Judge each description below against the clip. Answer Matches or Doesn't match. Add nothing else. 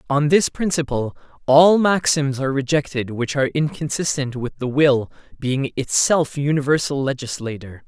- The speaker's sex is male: Matches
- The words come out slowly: Matches